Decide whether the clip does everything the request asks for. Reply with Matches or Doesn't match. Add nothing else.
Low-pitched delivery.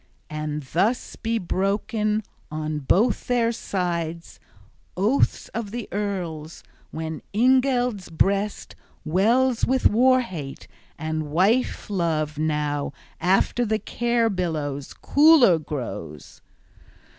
Doesn't match